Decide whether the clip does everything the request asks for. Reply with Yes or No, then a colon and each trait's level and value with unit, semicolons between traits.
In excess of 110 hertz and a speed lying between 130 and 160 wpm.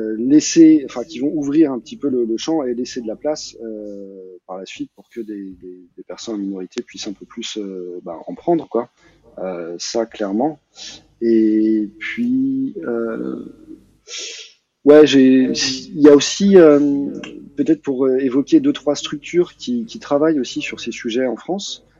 No: low, 135 Hz; average, 175 wpm